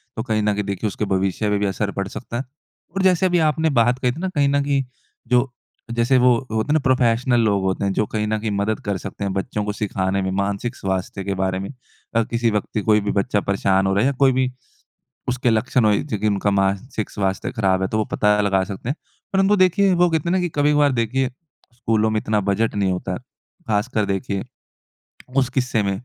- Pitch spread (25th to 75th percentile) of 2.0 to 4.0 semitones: No, average, 4.4 semitones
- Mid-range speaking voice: No, low, 110 Hz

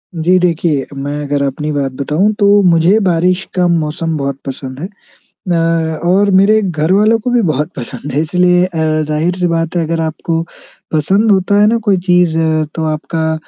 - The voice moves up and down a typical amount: Yes, average, 3.5 semitones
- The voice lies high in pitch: No, medium, 165 Hz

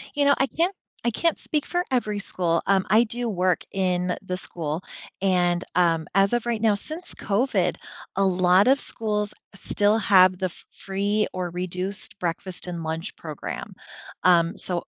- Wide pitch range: No, average, 3.3 semitones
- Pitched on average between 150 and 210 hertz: Yes, high, 190 Hz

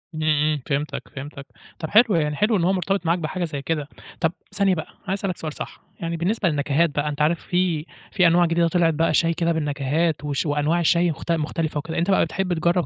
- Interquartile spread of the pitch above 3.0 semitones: No, average, 2.7 semitones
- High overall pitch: No, medium, 165 Hz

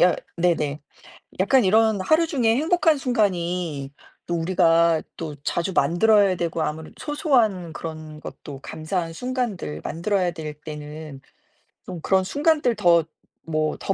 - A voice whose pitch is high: No, medium, 175 Hz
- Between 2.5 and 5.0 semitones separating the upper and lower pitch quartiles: No, wide, 5.6 semitones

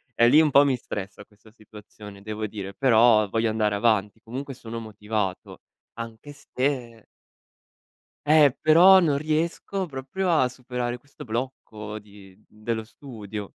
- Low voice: Yes, low, 115 Hz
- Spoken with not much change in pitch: No, average, 4.5 semitones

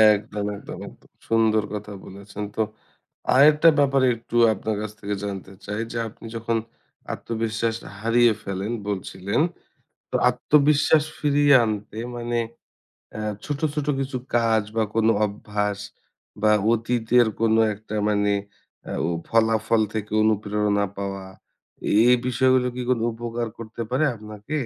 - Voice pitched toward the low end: Yes, low, 110 Hz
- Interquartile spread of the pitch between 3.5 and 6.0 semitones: No, narrow, 2.6 semitones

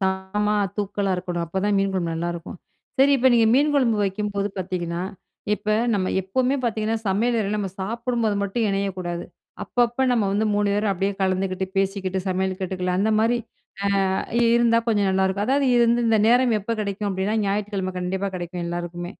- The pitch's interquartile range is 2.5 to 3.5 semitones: Yes, average, 2.9 semitones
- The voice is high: Yes, high, 200 Hz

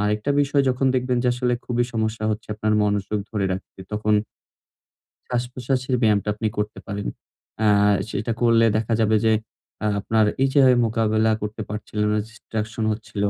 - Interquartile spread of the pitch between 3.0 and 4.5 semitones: No, narrow, 2.4 semitones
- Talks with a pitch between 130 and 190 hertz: No, low, 110 Hz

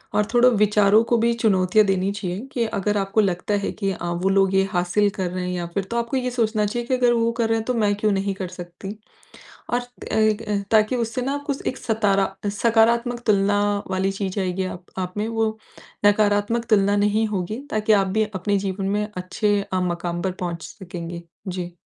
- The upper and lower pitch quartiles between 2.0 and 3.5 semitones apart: Yes, average, 2.9 semitones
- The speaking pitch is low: No, high, 205 Hz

